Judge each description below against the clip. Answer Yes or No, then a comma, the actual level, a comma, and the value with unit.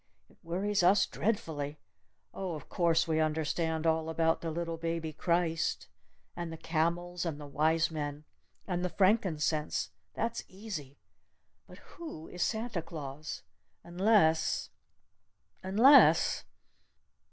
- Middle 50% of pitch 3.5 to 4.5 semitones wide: No, average, 2.7 semitones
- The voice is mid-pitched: Yes, medium, 165 Hz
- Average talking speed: No, slow, 120 wpm